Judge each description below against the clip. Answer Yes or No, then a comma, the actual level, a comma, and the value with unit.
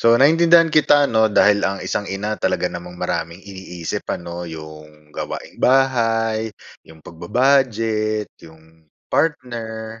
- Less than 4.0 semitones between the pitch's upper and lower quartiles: No, wide, 5.6 semitones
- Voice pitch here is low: Yes, low, 110 Hz